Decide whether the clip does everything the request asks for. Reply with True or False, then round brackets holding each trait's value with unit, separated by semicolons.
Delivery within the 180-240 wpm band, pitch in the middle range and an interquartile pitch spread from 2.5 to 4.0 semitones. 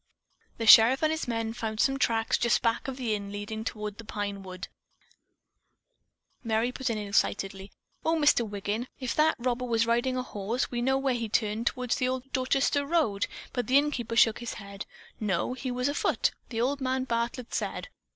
False (185 wpm; 235 Hz; 3.1 semitones)